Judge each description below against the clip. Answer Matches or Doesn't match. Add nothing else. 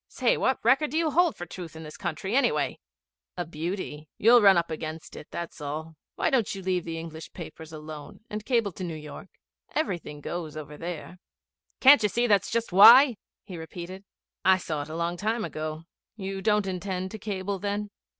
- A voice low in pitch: Doesn't match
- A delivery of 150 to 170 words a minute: Doesn't match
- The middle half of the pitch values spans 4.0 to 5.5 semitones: Matches